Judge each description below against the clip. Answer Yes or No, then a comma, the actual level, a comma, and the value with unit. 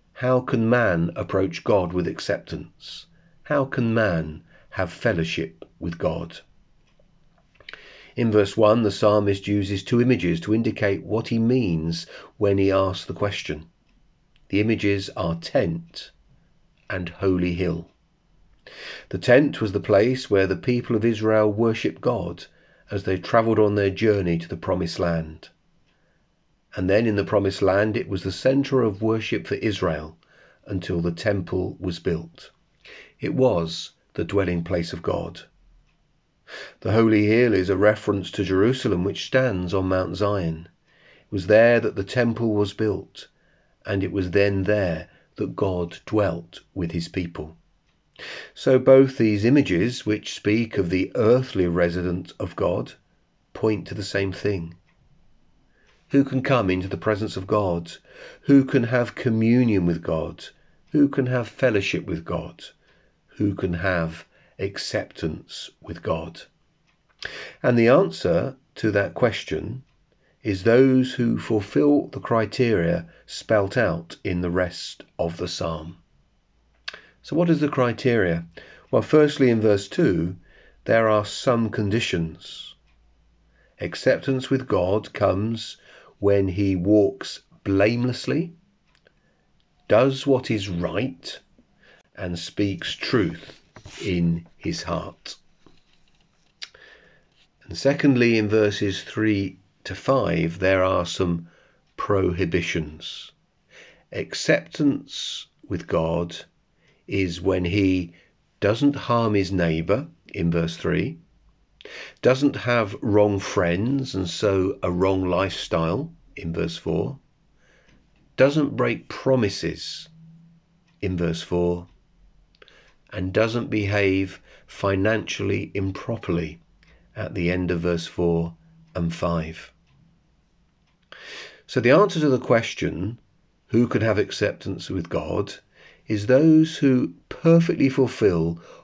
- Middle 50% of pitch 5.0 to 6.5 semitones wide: Yes, average, 5.3 semitones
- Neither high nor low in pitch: No, low, 100 Hz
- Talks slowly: Yes, slow, 125 wpm